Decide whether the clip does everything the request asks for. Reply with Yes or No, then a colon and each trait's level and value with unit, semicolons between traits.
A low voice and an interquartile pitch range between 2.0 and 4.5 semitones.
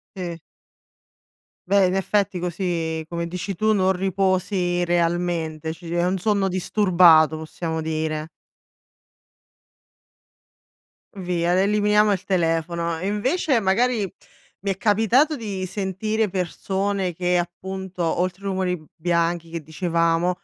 No: medium, 180 Hz; average, 2.7 semitones